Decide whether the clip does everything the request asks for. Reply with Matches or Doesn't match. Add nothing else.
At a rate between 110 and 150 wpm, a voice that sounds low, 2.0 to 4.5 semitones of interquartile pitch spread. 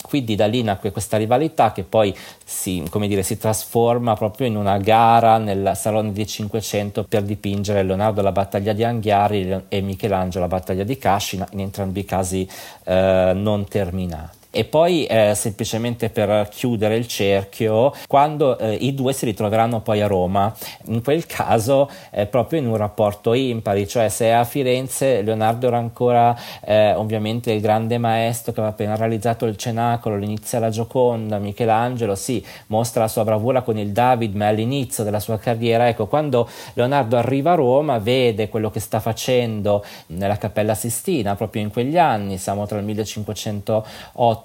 Doesn't match